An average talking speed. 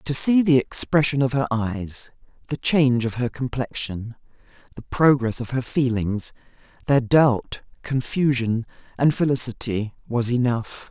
No: slow, 130 wpm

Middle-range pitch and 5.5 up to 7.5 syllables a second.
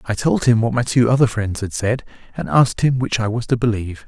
No: low, 115 Hz; 6.0 syllables/s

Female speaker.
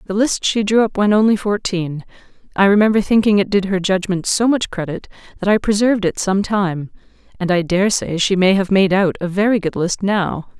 Yes: female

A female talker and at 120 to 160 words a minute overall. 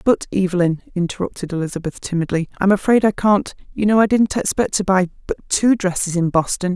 No: female; average, 185 wpm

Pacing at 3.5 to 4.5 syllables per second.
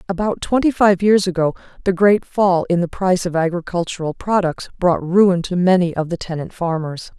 No: 5.2 syllables/s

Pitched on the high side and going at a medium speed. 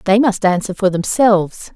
Yes: high, 200 Hz; average, 170 wpm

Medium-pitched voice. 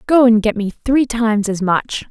No: high, 225 Hz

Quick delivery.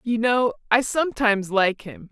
No: average, 170 wpm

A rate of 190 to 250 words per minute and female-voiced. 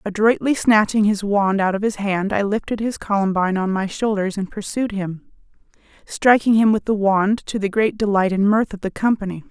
Yes: average, 200 wpm; female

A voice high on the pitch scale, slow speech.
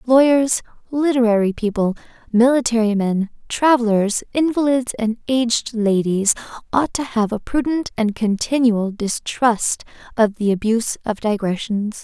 Yes: high, 230 Hz; slow, 115 wpm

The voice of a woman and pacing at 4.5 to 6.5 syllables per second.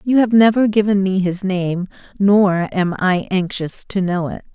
No: female; 4.3 syllables/s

